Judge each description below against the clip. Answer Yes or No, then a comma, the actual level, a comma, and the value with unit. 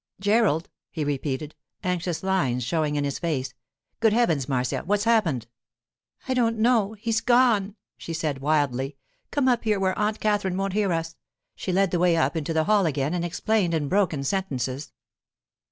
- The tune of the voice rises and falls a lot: Yes, wide, 6.1 semitones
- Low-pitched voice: No, medium, 175 Hz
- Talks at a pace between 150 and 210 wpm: Yes, average, 170 wpm